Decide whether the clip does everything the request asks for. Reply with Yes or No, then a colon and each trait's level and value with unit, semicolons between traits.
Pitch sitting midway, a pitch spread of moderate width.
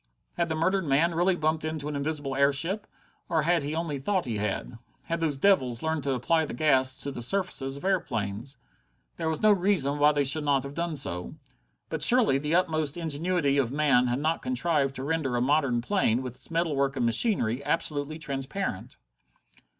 Yes: medium, 150 Hz; average, 3.7 semitones